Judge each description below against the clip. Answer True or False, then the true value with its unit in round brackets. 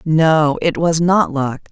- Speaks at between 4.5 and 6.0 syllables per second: False (3.2 syllables/s)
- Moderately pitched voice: True (155 Hz)